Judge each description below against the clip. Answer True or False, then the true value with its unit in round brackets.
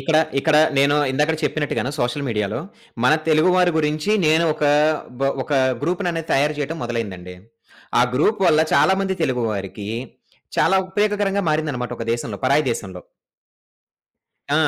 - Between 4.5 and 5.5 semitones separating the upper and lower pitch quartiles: True (5.2 semitones)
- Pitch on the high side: False (150 Hz)